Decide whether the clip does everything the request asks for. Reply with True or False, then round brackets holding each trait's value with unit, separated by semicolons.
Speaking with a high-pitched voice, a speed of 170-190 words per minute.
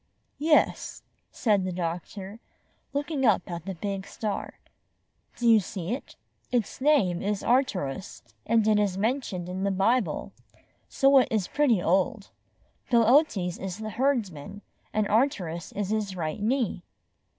False (210 Hz; 150 wpm)